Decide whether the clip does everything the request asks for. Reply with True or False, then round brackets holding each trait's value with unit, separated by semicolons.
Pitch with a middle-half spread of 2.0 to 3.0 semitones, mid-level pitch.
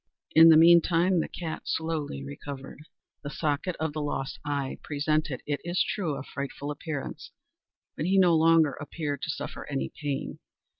True (2.5 semitones; 155 Hz)